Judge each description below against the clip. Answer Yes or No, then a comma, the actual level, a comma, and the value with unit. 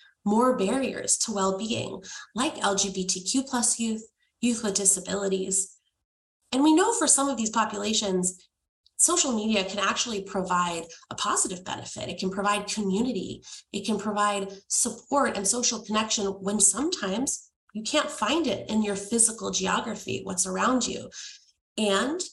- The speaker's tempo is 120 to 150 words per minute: Yes, average, 140 wpm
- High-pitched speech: Yes, high, 215 Hz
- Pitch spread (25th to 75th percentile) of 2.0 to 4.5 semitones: Yes, average, 3.9 semitones